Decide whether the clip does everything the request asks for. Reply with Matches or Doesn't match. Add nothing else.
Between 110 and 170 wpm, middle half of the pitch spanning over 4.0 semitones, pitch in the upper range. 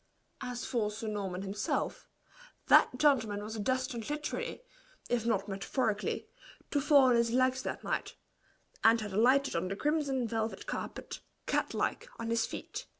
Doesn't match